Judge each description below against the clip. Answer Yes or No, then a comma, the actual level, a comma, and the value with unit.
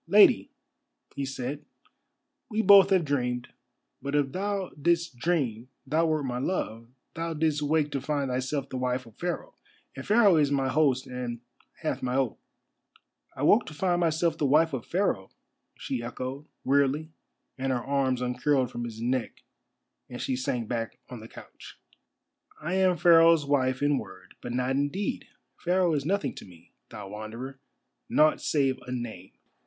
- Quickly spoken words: No, average, 165 wpm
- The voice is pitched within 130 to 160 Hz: Yes, medium, 140 Hz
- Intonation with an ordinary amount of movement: Yes, average, 4.4 semitones